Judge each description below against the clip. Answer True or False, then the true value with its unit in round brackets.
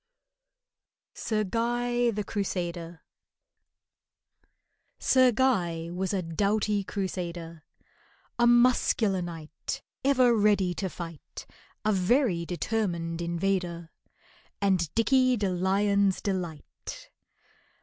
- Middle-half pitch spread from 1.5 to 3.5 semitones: False (4.8 semitones)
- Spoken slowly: True (90 wpm)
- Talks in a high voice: True (195 Hz)